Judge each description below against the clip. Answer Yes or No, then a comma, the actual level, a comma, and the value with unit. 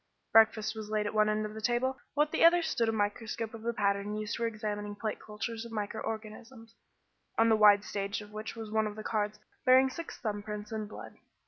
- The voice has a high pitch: Yes, high, 215 Hz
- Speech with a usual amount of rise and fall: No, narrow, 1.4 semitones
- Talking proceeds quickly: Yes, fast, 230 wpm